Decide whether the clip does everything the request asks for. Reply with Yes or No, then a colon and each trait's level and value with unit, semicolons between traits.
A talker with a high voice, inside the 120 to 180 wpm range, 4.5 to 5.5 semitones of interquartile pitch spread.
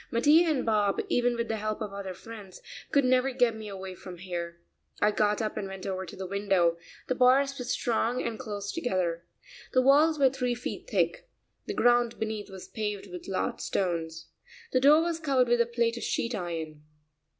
No: high, 220 Hz; average, 195 wpm; average, 4.8 semitones